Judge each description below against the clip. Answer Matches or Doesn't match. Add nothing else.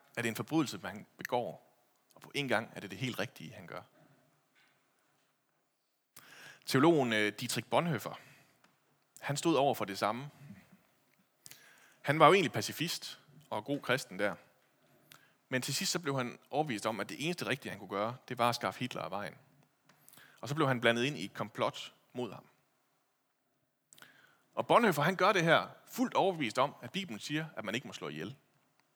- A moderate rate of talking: Matches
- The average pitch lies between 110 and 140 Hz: Matches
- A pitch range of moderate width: Matches